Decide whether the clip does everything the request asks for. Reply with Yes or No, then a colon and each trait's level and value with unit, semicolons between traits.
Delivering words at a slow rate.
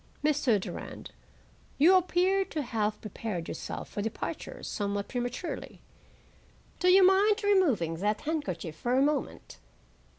Yes: slow, 125 wpm